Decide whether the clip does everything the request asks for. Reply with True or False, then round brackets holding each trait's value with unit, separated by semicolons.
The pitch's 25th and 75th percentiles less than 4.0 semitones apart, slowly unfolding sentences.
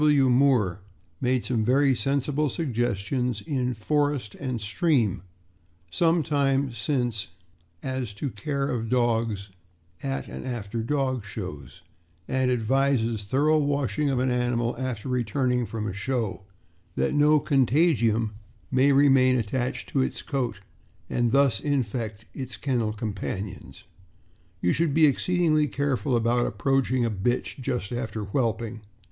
True (3.6 semitones; 130 wpm)